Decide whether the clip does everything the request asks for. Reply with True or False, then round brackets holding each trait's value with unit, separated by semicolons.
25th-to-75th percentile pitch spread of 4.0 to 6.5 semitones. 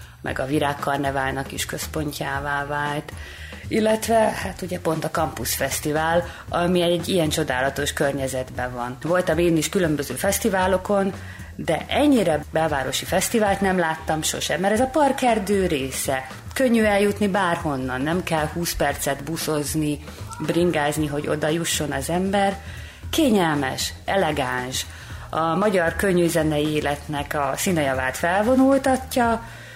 True (5.4 semitones)